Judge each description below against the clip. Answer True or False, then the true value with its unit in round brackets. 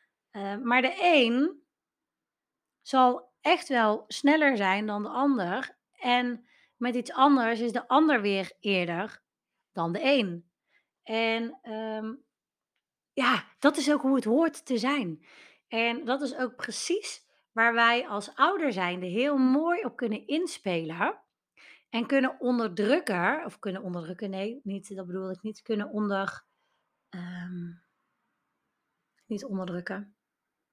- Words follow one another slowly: True (130 wpm)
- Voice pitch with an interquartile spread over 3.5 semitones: True (5.4 semitones)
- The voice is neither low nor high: False (235 Hz)